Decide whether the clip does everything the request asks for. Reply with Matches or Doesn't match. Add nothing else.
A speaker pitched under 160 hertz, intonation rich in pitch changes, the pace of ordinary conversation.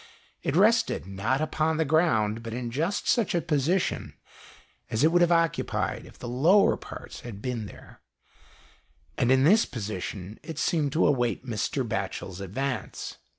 Matches